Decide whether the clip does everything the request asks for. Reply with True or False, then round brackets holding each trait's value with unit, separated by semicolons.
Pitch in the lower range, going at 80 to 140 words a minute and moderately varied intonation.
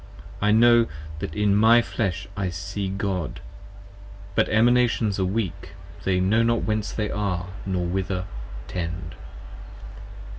True (100 Hz; 135 wpm; 3.1 semitones)